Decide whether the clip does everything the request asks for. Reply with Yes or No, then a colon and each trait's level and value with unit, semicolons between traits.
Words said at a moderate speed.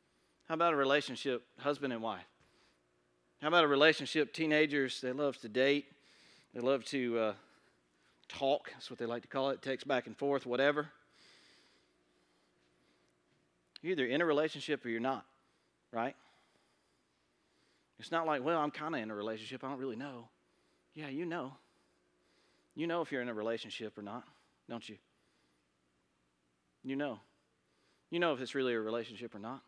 Yes: average, 165 wpm